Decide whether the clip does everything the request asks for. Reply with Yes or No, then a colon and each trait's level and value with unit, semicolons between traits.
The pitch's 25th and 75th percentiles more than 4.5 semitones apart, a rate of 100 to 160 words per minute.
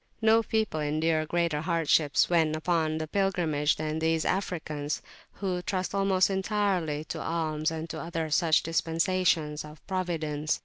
No: average, 3.0 semitones; average, 140 wpm